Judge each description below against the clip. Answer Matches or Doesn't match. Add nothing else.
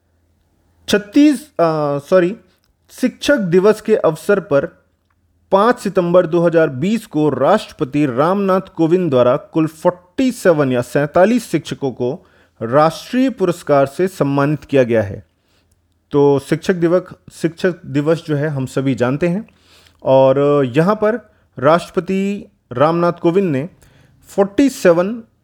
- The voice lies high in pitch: Doesn't match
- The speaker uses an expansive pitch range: Matches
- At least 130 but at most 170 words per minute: Doesn't match